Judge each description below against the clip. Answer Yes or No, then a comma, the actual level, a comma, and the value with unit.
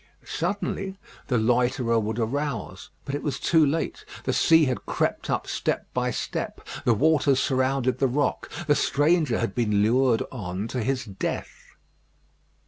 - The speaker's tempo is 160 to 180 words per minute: No, average, 150 wpm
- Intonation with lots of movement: No, average, 4.0 semitones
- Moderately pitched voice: No, low, 130 Hz